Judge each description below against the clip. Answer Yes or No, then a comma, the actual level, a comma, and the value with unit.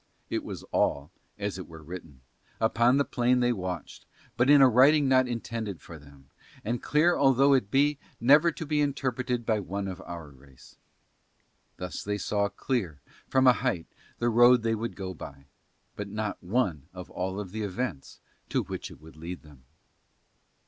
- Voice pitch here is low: Yes, low, 105 Hz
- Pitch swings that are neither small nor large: No, wide, 6.2 semitones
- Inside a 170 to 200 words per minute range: Yes, average, 175 wpm